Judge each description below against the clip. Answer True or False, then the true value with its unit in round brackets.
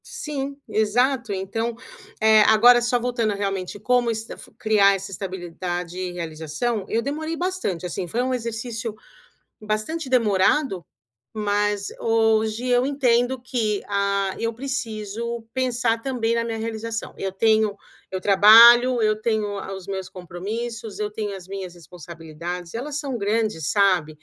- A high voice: True (220 Hz)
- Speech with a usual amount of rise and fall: True (3.6 semitones)